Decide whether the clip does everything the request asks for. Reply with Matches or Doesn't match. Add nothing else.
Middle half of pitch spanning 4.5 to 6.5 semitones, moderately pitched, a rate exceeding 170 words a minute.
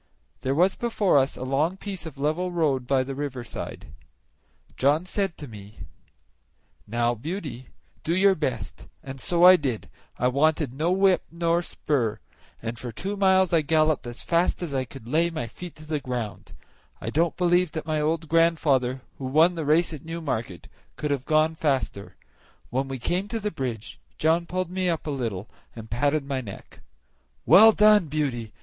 Matches